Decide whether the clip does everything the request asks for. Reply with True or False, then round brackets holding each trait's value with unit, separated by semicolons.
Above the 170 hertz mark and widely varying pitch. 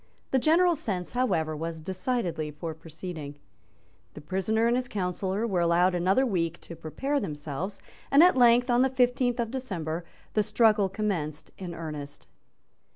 True (190 Hz; 6.9 semitones)